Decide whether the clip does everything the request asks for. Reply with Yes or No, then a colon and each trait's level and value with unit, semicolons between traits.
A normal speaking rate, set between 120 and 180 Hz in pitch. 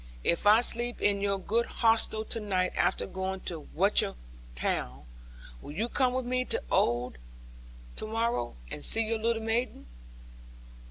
No: average, 155 wpm; high, 215 Hz